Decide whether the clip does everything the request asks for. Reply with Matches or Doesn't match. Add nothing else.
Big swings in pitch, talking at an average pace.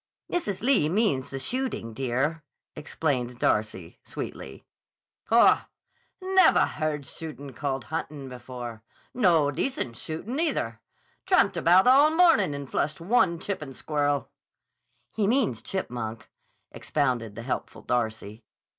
Doesn't match